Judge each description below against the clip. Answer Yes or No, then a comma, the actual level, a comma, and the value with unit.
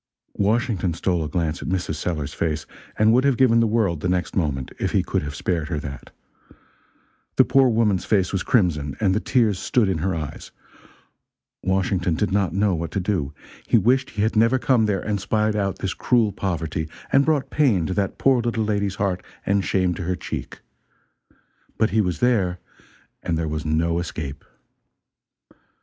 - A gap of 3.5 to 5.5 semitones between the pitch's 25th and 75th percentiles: Yes, average, 4.6 semitones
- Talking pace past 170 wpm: Yes, average, 185 wpm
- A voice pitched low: Yes, very low, 95 Hz